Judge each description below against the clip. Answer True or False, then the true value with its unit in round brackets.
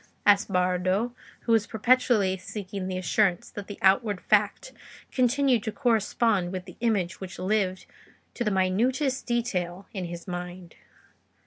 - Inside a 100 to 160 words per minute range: True (140 wpm)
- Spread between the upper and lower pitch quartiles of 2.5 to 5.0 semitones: True (4.0 semitones)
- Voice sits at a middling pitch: False (200 Hz)